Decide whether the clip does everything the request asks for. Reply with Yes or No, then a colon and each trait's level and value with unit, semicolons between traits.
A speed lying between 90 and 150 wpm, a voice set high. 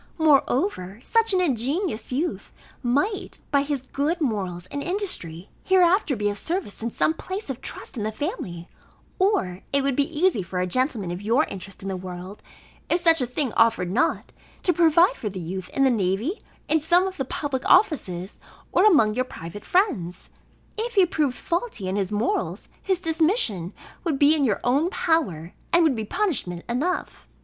No: average, 180 wpm; very high, 270 Hz